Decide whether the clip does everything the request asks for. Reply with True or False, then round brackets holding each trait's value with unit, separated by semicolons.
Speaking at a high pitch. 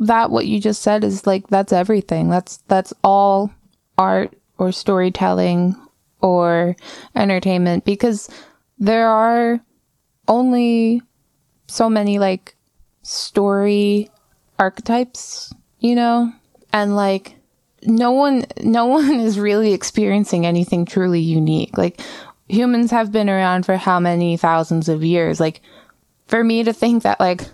True (205 Hz)